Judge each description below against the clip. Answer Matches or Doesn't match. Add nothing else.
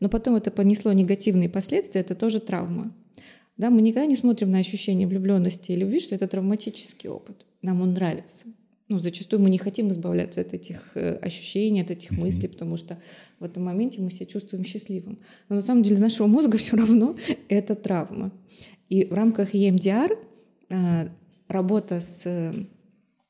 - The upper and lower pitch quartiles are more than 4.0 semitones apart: Doesn't match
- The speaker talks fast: Matches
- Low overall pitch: Doesn't match